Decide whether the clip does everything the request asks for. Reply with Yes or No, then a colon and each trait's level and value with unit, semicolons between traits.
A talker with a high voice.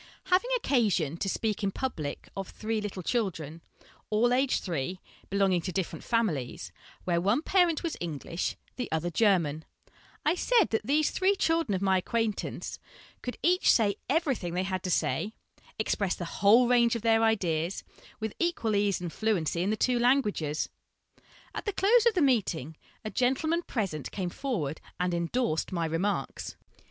Yes: high, 210 Hz